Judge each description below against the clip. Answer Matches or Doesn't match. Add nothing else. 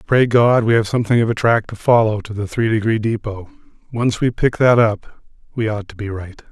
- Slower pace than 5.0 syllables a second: Doesn't match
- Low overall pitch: Matches